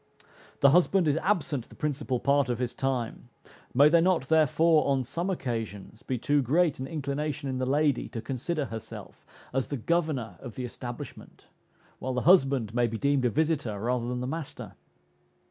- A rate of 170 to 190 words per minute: Yes, average, 180 wpm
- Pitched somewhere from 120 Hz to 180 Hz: Yes, low, 135 Hz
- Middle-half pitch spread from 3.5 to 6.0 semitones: Yes, average, 3.9 semitones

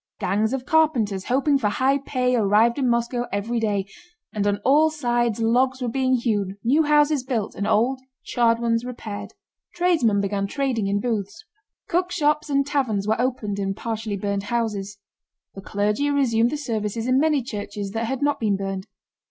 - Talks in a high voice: Yes, high, 235 Hz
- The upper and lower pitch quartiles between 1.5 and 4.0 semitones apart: No, average, 4.5 semitones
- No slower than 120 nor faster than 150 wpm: No, average, 170 wpm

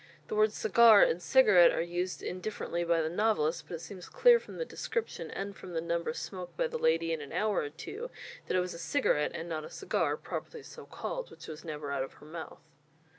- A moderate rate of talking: No, fast, 230 wpm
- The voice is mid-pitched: Yes, medium, 175 Hz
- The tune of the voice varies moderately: No, wide, 6.3 semitones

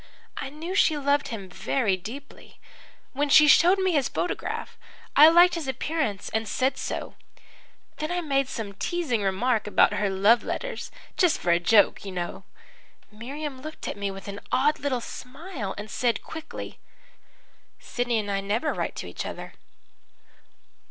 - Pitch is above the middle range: Yes, very high, 255 Hz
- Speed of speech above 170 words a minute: No, average, 160 wpm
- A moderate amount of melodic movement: No, wide, 6.9 semitones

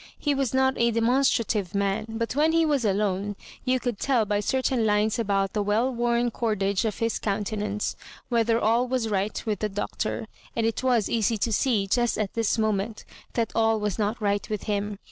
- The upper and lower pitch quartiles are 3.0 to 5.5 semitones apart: No, narrow, 2.5 semitones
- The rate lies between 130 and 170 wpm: No, average, 195 wpm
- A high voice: Yes, high, 220 Hz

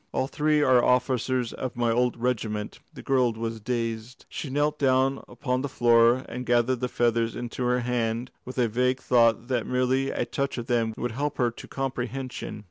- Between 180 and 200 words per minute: Yes, average, 185 wpm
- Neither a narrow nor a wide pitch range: No, narrow, 1.9 semitones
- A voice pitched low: Yes, low, 125 Hz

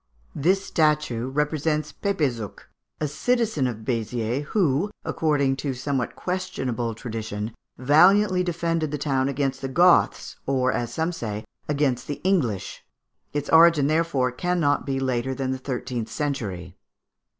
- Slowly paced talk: Yes, slow, 130 wpm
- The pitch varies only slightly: No, average, 4.4 semitones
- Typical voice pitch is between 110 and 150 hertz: Yes, medium, 140 Hz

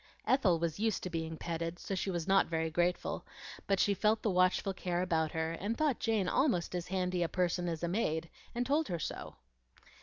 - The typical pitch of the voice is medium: Yes, medium, 180 Hz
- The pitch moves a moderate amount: Yes, average, 3.3 semitones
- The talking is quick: Yes, fast, 210 wpm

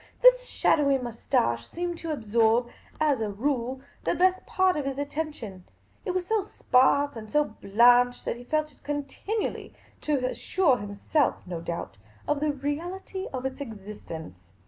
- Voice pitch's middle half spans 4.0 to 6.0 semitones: Yes, wide, 5.6 semitones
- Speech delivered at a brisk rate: No, average, 155 wpm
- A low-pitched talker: No, very high, 275 Hz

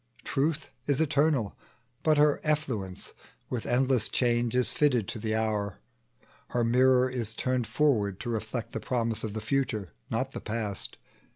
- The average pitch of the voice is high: No, low, 120 Hz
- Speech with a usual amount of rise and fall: Yes, average, 3.9 semitones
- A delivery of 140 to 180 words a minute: Yes, average, 155 wpm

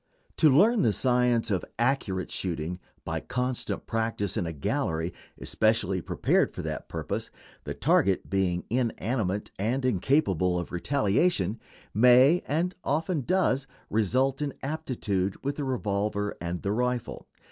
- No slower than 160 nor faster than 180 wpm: No, slow, 135 wpm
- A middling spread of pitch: No, wide, 5.8 semitones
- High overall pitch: No, low, 115 Hz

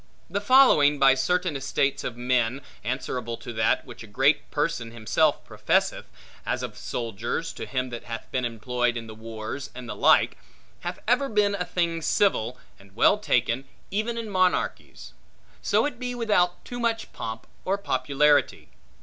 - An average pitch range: No, wide, 8.1 semitones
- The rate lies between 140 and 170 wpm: Yes, average, 165 wpm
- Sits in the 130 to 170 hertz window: Yes, low, 135 Hz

